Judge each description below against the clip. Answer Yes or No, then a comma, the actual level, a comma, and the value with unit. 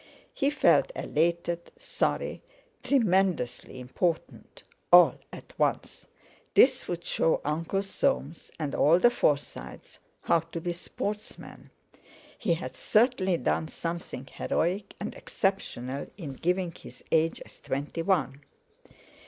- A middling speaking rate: No, slow, 115 wpm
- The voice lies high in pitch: No, medium, 170 Hz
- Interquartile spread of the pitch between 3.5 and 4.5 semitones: Yes, average, 3.8 semitones